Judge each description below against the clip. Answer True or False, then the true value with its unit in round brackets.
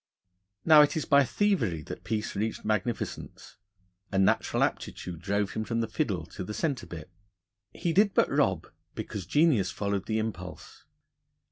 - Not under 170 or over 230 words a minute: False (155 wpm)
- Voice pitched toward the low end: True (110 Hz)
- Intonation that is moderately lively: False (6.7 semitones)